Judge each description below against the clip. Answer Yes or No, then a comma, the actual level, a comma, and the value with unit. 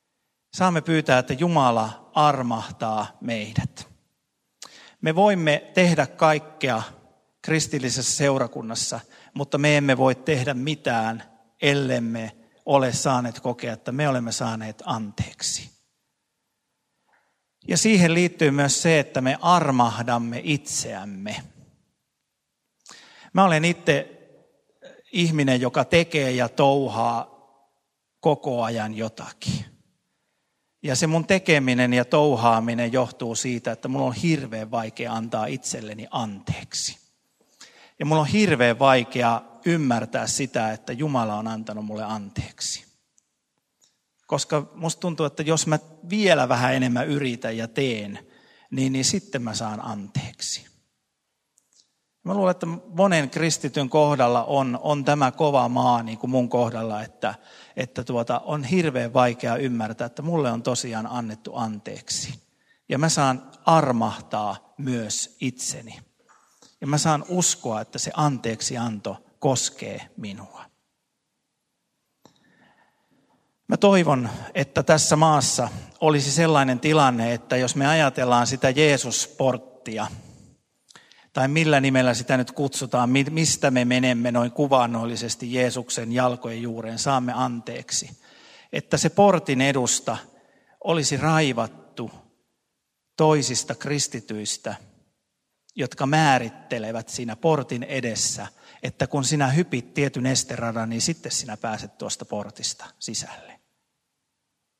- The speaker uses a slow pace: No, average, 110 wpm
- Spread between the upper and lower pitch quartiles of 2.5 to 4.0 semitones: No, average, 4.4 semitones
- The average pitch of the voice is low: Yes, low, 130 Hz